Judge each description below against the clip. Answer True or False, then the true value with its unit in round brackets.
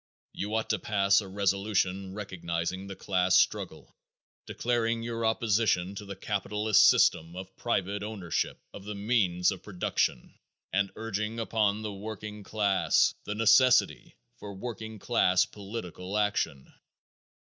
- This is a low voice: True (100 Hz)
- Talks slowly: True (130 wpm)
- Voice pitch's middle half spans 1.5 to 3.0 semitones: True (2.4 semitones)